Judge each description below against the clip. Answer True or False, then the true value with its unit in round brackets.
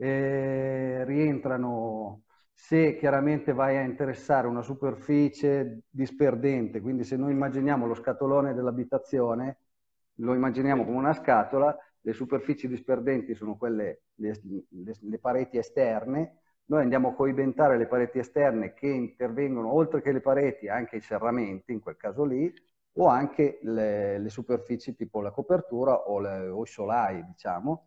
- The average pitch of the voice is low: True (130 Hz)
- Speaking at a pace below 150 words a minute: True (140 wpm)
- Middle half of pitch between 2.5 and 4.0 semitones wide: True (3.1 semitones)